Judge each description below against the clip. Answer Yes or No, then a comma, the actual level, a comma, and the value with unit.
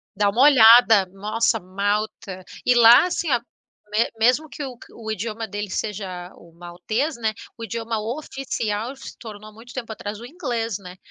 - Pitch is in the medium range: No, high, 225 Hz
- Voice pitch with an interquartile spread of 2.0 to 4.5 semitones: Yes, average, 2.9 semitones